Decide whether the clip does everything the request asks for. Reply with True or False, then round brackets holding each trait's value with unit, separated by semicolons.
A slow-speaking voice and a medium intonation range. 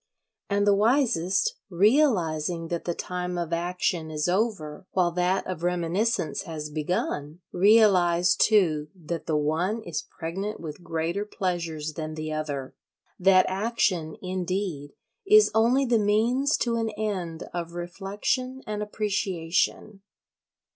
True (125 wpm; 4.2 semitones)